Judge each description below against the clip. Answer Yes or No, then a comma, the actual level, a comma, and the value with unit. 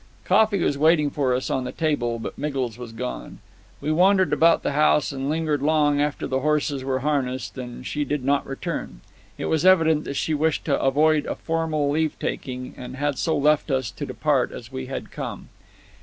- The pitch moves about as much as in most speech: Yes, average, 3.0 semitones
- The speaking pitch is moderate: Yes, medium, 145 Hz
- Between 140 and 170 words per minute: No, average, 200 wpm